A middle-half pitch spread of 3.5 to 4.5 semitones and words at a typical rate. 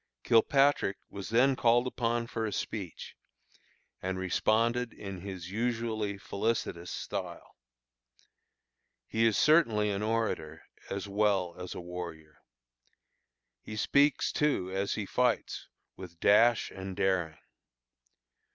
No: average, 3.8 semitones; slow, 115 wpm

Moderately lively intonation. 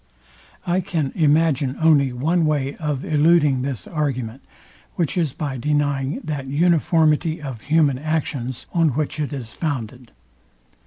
Yes: average, 3.1 semitones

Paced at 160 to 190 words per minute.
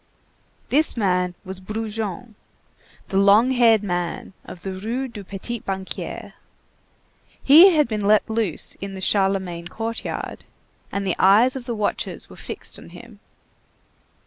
No: average, 140 wpm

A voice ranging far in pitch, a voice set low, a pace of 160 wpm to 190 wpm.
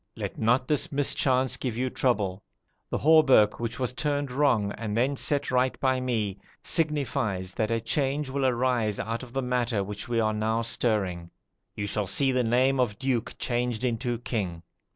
No: average, 3.5 semitones; low, 120 Hz; average, 175 wpm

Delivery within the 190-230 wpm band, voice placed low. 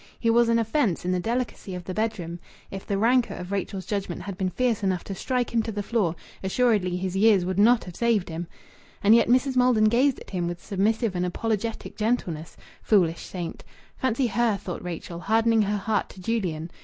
No: fast, 205 wpm; high, 205 Hz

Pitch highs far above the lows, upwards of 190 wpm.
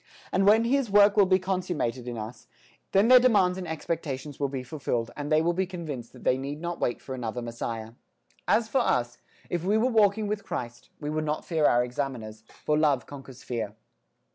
Yes: wide, 7.5 semitones; fast, 205 wpm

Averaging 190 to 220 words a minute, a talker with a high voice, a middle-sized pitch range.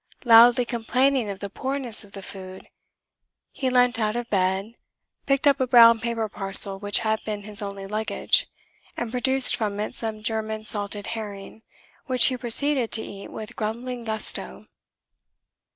No: average, 155 wpm; high, 220 Hz; average, 3.1 semitones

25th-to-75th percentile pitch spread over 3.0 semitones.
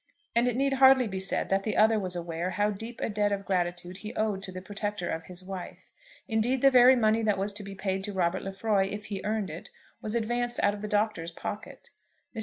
No: average, 2.7 semitones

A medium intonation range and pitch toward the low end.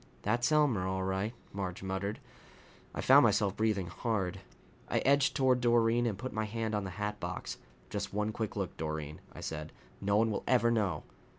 Yes: average, 3.5 semitones; low, 105 Hz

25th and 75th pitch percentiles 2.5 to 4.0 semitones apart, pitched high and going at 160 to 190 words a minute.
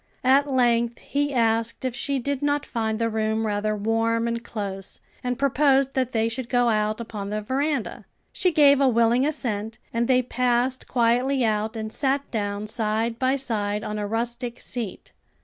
Yes: average, 3.0 semitones; high, 235 Hz; average, 175 wpm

